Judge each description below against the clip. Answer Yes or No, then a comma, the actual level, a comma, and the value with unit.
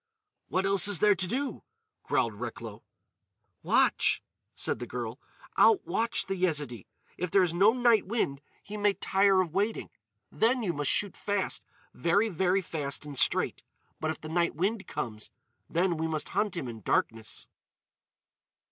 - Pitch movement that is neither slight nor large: Yes, average, 4.5 semitones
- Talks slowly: No, average, 155 wpm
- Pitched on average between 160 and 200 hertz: Yes, medium, 185 Hz